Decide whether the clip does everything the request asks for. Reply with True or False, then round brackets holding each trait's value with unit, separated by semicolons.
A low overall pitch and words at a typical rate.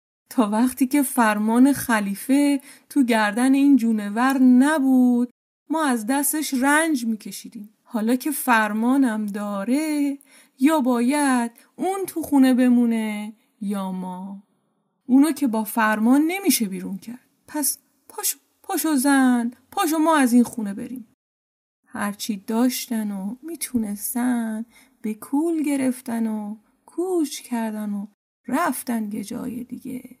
False (250 Hz; 115 wpm)